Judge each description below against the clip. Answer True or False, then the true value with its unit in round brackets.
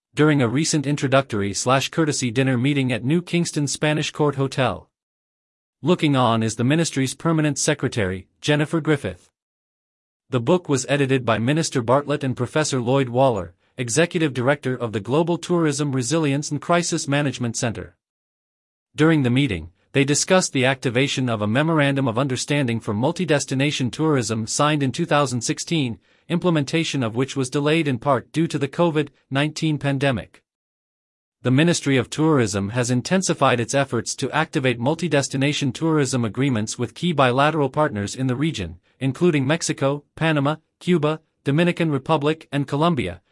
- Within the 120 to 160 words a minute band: True (145 wpm)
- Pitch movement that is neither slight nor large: True (3.5 semitones)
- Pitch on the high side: False (140 Hz)